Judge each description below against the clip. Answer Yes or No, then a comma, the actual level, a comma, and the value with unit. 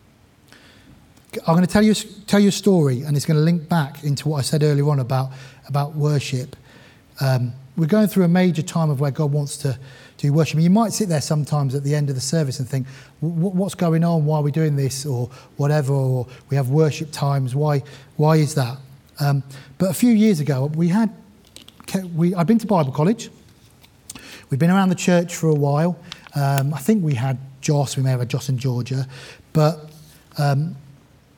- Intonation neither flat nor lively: Yes, average, 3.7 semitones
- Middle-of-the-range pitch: Yes, medium, 150 Hz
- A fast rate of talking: Yes, fast, 210 wpm